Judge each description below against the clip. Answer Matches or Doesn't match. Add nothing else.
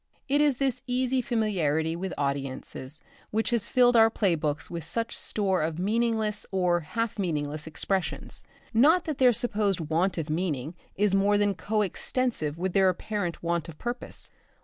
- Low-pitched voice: Doesn't match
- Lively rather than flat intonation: Matches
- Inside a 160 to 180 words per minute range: Matches